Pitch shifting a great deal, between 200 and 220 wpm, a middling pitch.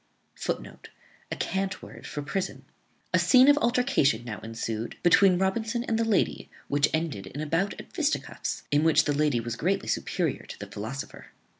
No: wide, 8.3 semitones; average, 180 wpm; medium, 160 Hz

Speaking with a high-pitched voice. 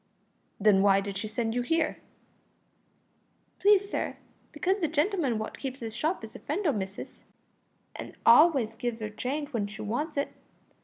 Yes: high, 245 Hz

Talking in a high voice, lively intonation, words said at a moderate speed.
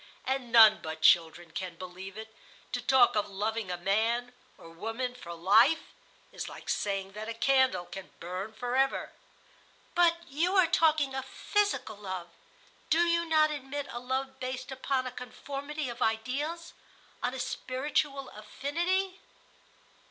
Yes: very high, 250 Hz; wide, 5.7 semitones; average, 145 wpm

